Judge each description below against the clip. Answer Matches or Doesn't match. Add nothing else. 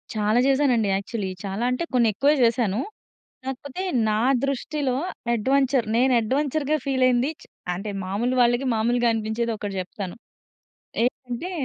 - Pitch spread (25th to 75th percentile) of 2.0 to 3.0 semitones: Doesn't match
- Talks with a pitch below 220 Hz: Doesn't match